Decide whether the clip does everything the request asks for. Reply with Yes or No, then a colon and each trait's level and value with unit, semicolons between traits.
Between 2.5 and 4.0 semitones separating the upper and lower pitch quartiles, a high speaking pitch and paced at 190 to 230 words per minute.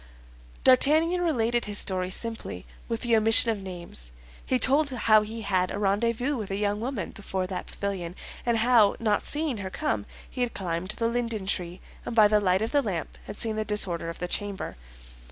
Yes: average, 3.7 semitones; high, 215 Hz; average, 195 wpm